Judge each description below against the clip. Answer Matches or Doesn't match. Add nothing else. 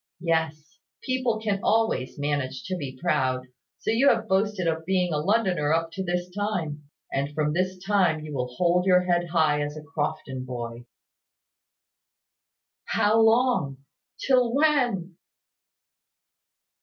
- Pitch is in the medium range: Matches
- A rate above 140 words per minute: Doesn't match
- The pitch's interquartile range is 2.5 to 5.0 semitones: Doesn't match